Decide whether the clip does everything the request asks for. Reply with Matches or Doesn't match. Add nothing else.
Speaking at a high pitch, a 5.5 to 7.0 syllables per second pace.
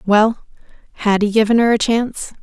Matches